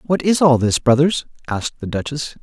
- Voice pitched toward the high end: No, medium, 140 Hz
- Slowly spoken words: No, average, 200 wpm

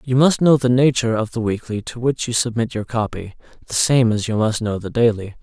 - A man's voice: Yes, male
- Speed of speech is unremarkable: No, fast, 245 wpm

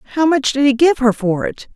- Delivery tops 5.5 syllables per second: Yes, 5.7 syllables/s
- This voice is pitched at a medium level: No, very high, 265 Hz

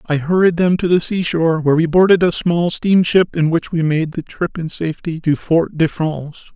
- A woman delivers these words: No, male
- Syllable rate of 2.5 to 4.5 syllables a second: No, 5.3 syllables/s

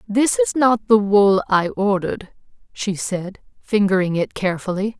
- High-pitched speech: Yes, high, 200 Hz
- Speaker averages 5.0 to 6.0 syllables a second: No, 4.6 syllables/s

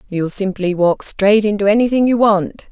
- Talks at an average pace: Yes, average, 175 wpm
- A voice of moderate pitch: No, high, 205 Hz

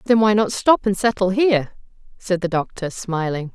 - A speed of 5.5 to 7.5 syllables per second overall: No, 5.1 syllables/s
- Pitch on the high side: Yes, high, 195 Hz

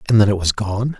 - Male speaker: Yes, male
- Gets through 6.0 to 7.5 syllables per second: Yes, 6.2 syllables/s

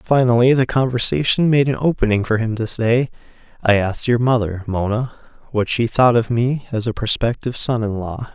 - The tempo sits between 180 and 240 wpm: Yes, average, 185 wpm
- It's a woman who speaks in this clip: No, male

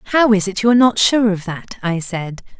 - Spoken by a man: No, female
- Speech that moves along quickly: Yes, fast, 255 wpm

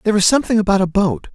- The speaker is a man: Yes, male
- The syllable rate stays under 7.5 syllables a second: No, 8.3 syllables/s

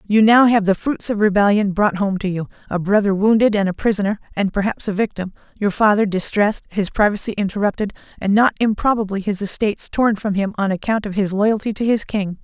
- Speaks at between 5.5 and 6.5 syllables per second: Yes, 5.9 syllables/s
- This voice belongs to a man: No, female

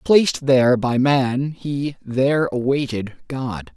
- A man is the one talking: Yes, male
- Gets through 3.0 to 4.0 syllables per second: Yes, 3.7 syllables/s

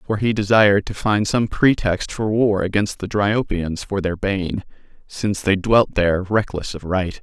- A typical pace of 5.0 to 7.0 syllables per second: No, 4.6 syllables/s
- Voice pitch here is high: No, low, 100 Hz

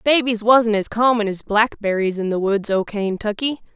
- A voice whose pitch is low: No, high, 215 Hz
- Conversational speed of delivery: Yes, average, 175 wpm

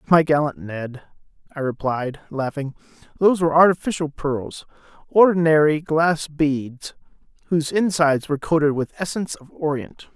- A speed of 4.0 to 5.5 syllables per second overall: Yes, 5.1 syllables/s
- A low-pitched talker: No, medium, 150 Hz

